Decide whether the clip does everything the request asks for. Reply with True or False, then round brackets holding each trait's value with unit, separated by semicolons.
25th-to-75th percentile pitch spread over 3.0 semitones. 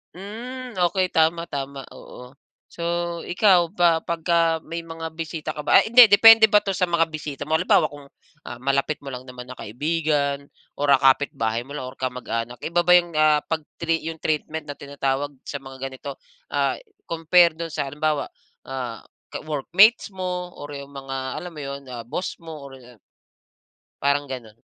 True (3.7 semitones)